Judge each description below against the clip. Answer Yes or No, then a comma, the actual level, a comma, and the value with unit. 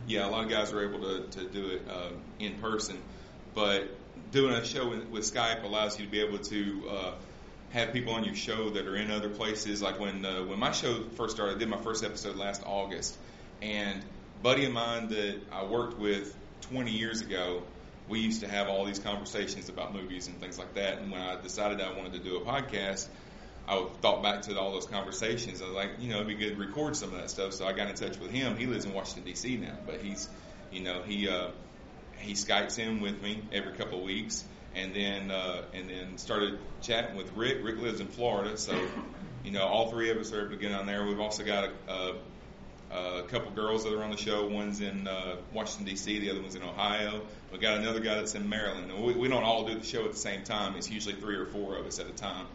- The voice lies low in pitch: Yes, low, 105 Hz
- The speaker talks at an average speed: No, fast, 240 wpm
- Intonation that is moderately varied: No, narrow, 2.0 semitones